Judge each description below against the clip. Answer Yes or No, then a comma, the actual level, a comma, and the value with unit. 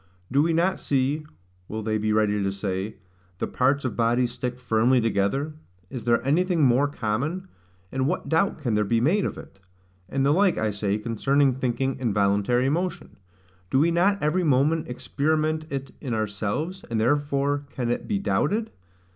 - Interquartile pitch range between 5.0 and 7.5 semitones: Yes, wide, 5.4 semitones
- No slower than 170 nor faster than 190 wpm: Yes, average, 175 wpm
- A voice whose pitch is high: No, low, 130 Hz